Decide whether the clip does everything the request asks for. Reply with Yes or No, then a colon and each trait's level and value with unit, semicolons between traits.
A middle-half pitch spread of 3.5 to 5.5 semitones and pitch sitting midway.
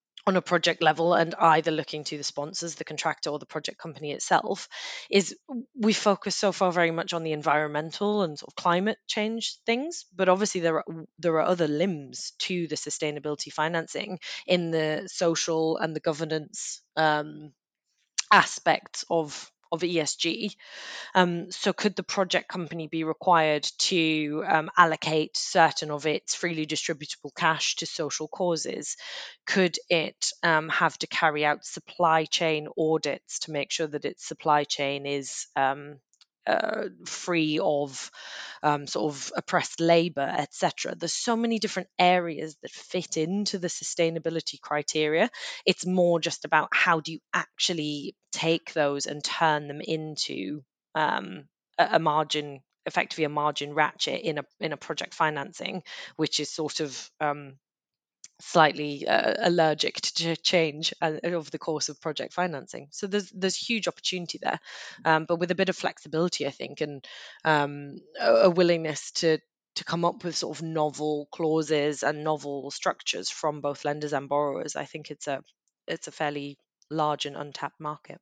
No: narrow, 2.5 semitones; medium, 160 Hz